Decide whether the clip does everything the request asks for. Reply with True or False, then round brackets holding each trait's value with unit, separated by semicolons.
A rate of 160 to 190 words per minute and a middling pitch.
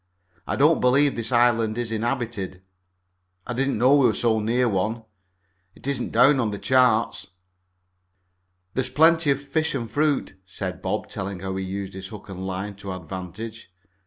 False (175 wpm; 115 Hz)